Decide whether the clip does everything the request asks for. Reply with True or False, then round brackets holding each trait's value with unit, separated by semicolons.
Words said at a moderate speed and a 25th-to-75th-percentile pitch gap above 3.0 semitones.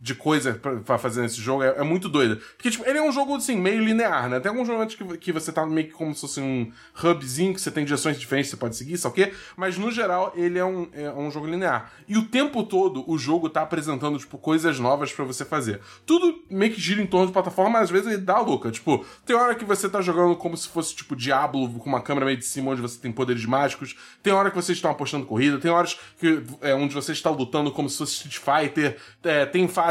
False (255 wpm; 5.5 semitones)